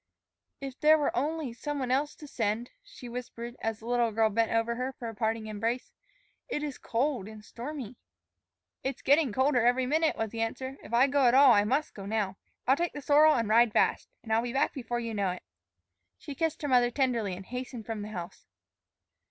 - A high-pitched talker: Yes, high, 245 Hz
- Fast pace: Yes, fast, 215 wpm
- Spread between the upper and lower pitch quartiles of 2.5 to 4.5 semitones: Yes, average, 3.5 semitones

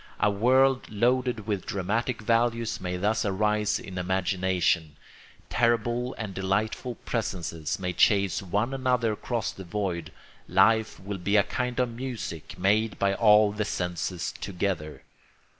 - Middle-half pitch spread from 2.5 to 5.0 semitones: Yes, average, 3.7 semitones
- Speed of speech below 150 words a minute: Yes, slow, 135 wpm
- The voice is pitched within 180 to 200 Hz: No, low, 105 Hz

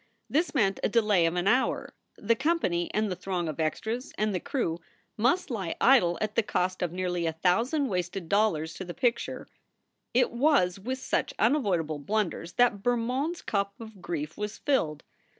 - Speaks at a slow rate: No, average, 180 wpm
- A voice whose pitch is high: Yes, high, 200 Hz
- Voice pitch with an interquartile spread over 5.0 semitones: Yes, wide, 5.6 semitones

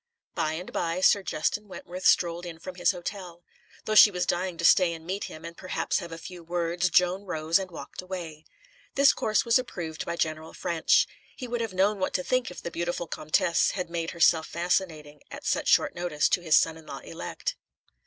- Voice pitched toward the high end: No, medium, 175 Hz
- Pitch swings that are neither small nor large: No, narrow, 2.2 semitones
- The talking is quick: Yes, fast, 210 wpm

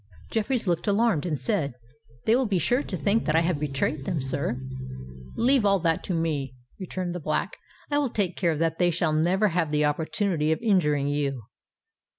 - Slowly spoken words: No, average, 190 wpm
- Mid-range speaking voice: Yes, medium, 170 Hz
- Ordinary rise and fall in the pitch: Yes, average, 5.0 semitones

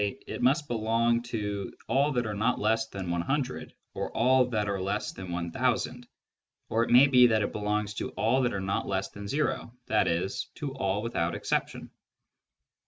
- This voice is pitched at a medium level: No, low, 110 Hz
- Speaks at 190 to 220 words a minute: No, average, 175 wpm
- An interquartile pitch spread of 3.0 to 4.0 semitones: Yes, average, 3.7 semitones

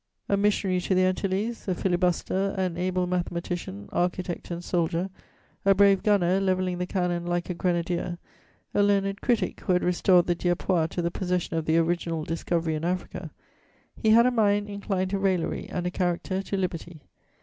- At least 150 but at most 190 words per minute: Yes, average, 175 wpm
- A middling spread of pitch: No, narrow, 2.0 semitones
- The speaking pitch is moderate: Yes, medium, 180 Hz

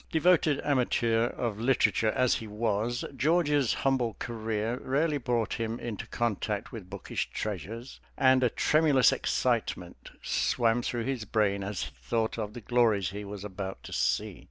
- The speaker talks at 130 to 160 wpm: Yes, average, 155 wpm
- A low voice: Yes, low, 115 Hz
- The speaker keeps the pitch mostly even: No, average, 3.6 semitones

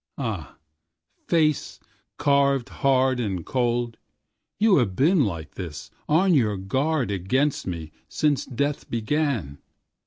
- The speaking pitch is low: Yes, low, 130 Hz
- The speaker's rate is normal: No, slow, 100 wpm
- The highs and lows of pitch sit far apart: Yes, wide, 6.6 semitones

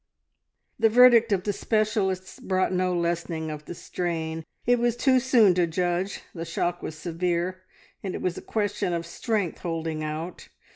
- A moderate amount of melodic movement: Yes, average, 3.9 semitones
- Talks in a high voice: No, medium, 180 Hz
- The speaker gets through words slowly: No, average, 165 wpm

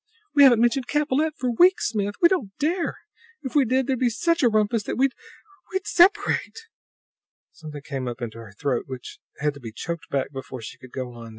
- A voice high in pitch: Yes, high, 230 Hz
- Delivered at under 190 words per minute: No, fast, 205 wpm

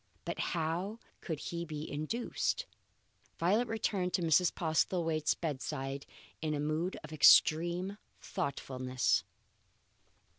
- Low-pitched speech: No, medium, 160 Hz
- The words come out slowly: Yes, slow, 105 wpm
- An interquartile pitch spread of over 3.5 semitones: No, average, 3.1 semitones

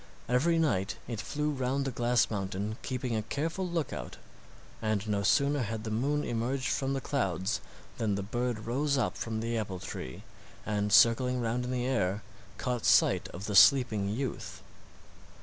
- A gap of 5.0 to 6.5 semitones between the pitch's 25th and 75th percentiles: No, average, 4.2 semitones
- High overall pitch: No, low, 120 Hz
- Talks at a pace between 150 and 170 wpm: Yes, average, 165 wpm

